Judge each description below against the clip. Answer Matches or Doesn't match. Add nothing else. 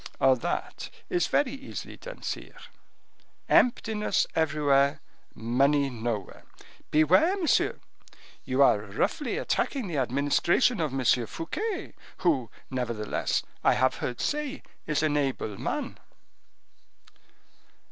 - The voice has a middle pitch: Matches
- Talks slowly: Matches